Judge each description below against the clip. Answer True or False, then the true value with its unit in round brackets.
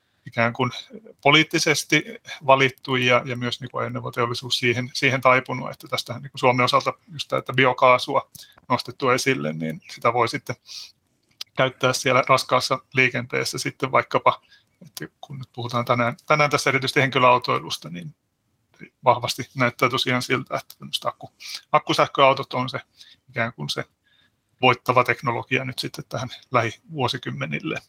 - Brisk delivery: False (130 wpm)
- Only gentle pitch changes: True (1.7 semitones)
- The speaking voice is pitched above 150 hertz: False (130 Hz)